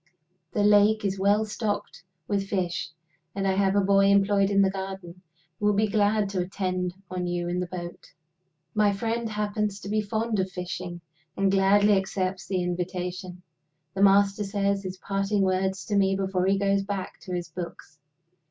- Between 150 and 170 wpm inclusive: No, average, 180 wpm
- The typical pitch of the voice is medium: No, high, 195 Hz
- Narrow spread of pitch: Yes, narrow, 1.7 semitones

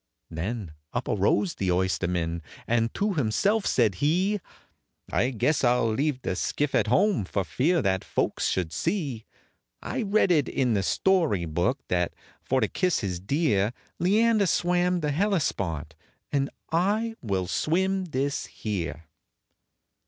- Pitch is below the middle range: Yes, low, 130 Hz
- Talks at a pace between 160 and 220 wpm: No, average, 145 wpm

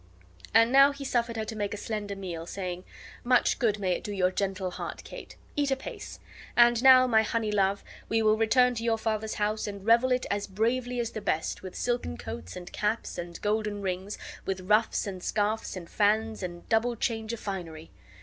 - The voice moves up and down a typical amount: Yes, average, 3.2 semitones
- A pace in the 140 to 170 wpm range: No, average, 200 wpm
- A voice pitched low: No, high, 215 Hz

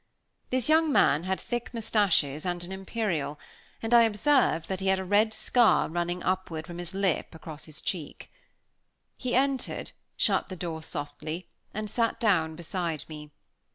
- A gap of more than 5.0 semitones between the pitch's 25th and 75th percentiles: Yes, wide, 5.4 semitones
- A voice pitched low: No, medium, 185 Hz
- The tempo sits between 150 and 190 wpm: Yes, average, 160 wpm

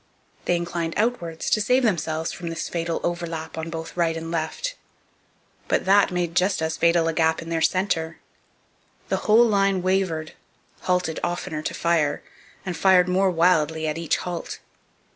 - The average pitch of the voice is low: No, medium, 170 Hz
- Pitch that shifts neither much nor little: No, narrow, 2.3 semitones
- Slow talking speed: No, average, 160 wpm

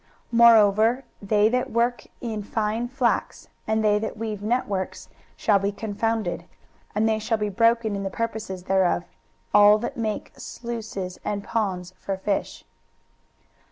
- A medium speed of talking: Yes, average, 150 wpm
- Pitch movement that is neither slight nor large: No, narrow, 2.3 semitones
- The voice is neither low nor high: No, high, 215 Hz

